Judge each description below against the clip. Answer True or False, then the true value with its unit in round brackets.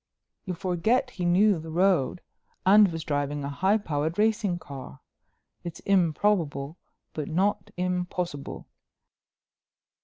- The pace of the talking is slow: True (115 wpm)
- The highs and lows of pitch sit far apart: False (4.2 semitones)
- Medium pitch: True (175 Hz)